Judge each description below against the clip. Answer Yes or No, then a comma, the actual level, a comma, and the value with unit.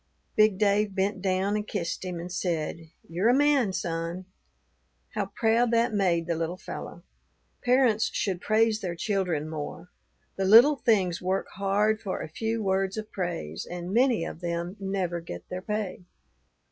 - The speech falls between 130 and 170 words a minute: Yes, average, 160 wpm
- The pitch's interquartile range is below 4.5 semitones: Yes, average, 3.7 semitones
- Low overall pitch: No, high, 190 Hz